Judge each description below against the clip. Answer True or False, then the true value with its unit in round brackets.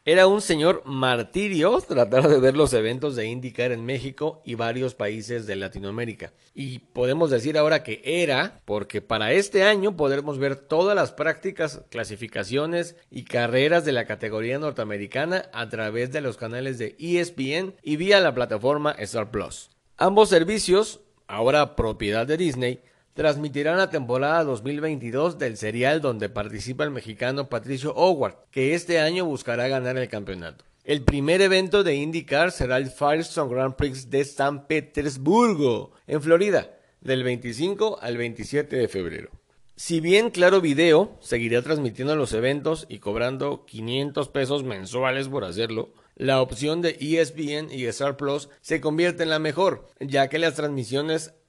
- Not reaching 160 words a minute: True (150 wpm)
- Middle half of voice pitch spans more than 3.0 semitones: True (4.7 semitones)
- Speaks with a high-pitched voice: False (140 Hz)